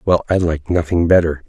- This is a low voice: Yes, very low, 85 Hz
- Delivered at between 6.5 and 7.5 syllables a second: No, 5.4 syllables/s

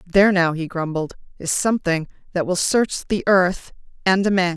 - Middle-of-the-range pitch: Yes, medium, 180 Hz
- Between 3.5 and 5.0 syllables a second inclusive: Yes, 4.9 syllables/s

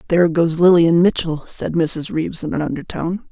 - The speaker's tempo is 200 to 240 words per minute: No, average, 180 wpm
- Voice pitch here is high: No, medium, 165 Hz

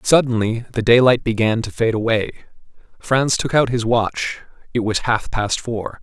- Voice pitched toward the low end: Yes, low, 115 Hz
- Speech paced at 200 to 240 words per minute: No, average, 160 wpm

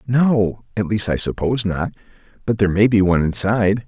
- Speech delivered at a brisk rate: No, average, 185 wpm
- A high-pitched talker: No, low, 105 Hz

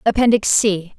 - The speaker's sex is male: No, female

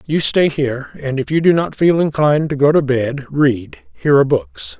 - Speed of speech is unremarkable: No, fast, 215 wpm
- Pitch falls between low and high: Yes, medium, 145 Hz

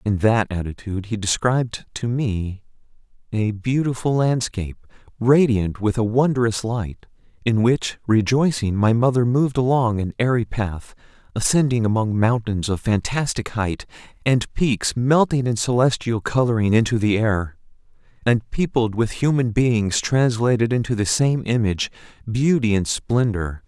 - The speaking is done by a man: Yes, male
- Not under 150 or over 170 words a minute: No, slow, 135 wpm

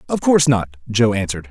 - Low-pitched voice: Yes, low, 120 Hz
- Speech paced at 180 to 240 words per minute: Yes, average, 200 wpm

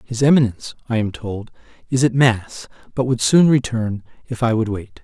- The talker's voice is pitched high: No, low, 120 Hz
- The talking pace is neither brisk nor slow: Yes, average, 190 wpm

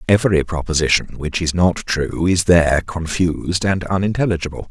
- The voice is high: No, very low, 85 Hz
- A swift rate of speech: No, average, 140 wpm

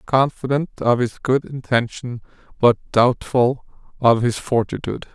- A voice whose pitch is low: Yes, low, 125 Hz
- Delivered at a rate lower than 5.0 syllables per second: Yes, 4.5 syllables/s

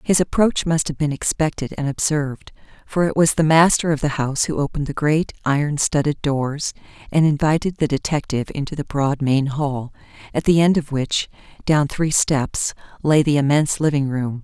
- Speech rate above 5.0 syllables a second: Yes, 5.2 syllables/s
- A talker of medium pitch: Yes, medium, 145 Hz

